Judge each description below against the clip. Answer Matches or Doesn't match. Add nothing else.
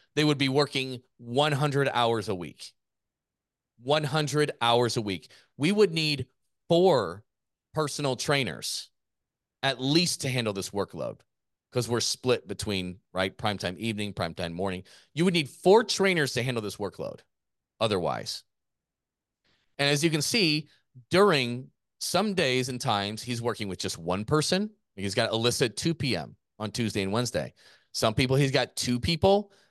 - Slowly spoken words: Doesn't match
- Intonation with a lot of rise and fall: Matches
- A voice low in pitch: Matches